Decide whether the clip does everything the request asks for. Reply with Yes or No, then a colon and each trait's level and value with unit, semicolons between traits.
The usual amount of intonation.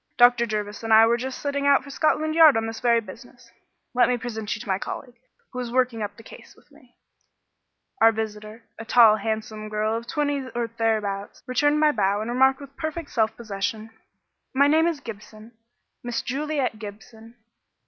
Yes: average, 3.4 semitones